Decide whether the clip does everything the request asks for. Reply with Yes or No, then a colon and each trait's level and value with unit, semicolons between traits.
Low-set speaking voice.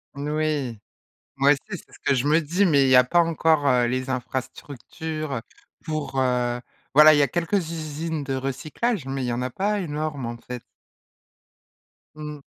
No: medium, 145 Hz